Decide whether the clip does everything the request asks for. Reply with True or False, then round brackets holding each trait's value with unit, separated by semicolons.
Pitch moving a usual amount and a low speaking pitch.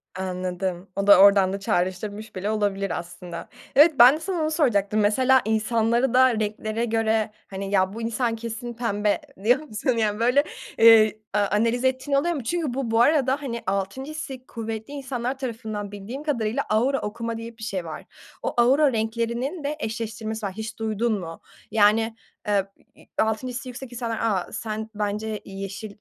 False (3.3 semitones; 225 Hz)